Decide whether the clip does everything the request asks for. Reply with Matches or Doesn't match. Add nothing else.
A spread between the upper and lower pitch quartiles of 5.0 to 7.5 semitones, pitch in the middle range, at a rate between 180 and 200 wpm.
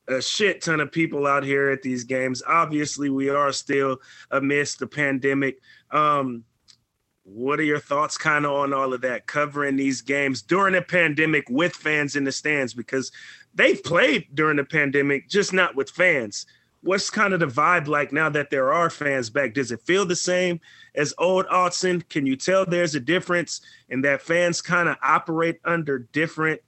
Doesn't match